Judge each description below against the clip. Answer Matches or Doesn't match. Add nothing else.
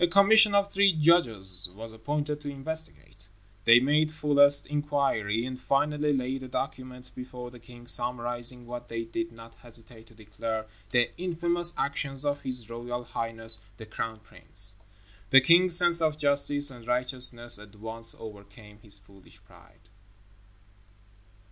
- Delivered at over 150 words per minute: Doesn't match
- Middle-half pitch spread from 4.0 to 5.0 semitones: Matches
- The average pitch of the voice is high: Doesn't match